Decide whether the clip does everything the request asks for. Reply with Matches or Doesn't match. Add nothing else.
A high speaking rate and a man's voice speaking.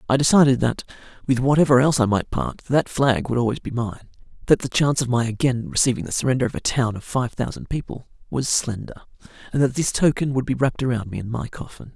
Matches